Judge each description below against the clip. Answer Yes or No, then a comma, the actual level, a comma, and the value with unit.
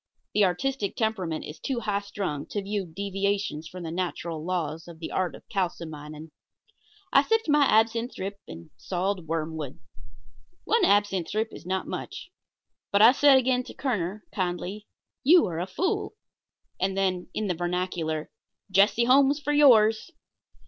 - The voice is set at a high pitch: Yes, high, 195 Hz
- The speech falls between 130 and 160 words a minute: Yes, average, 155 wpm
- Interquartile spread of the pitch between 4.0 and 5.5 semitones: Yes, average, 4.5 semitones